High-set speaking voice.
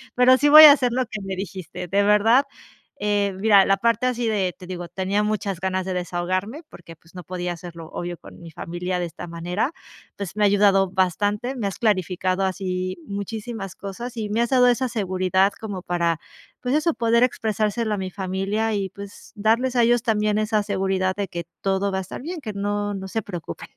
Yes: high, 200 Hz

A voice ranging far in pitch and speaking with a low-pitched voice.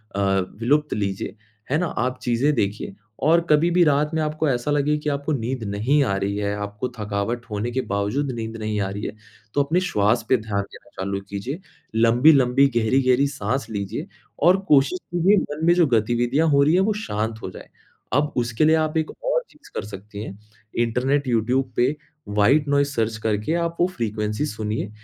Yes: wide, 5.8 semitones; low, 125 Hz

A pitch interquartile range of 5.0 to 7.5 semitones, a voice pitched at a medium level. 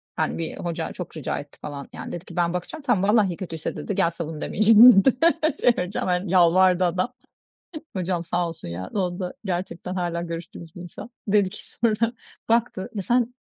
No: average, 3.4 semitones; medium, 180 Hz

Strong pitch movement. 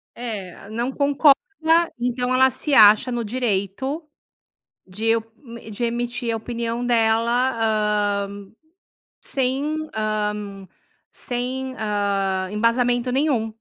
No: average, 3.1 semitones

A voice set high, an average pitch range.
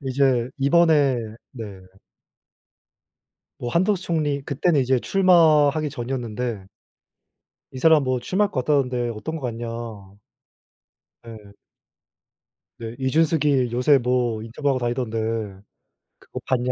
No: low, 130 Hz; average, 3.9 semitones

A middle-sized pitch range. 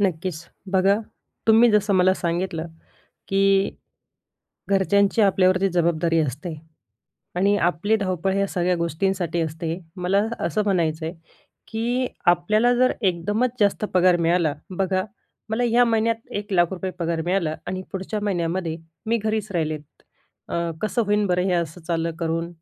Yes: average, 3.2 semitones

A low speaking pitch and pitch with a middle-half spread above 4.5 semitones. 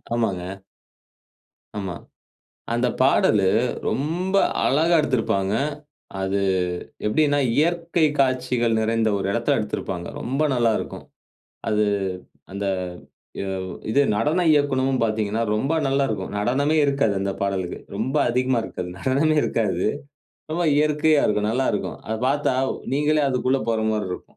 Yes: low, 125 Hz; average, 5.3 semitones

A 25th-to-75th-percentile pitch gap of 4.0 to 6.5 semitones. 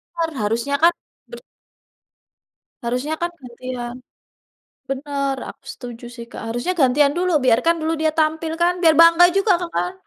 Yes: average, 5.1 semitones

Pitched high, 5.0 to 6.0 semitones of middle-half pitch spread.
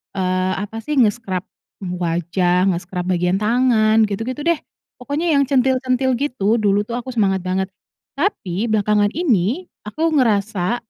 Yes: high, 215 Hz; wide, 5.4 semitones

